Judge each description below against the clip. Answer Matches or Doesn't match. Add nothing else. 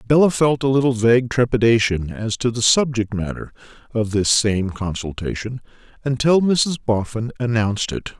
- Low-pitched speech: Matches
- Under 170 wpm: Matches